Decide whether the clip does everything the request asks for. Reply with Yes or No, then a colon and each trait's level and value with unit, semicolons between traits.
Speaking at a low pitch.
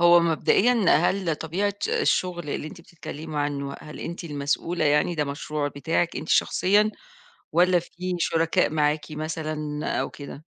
No: medium, 160 Hz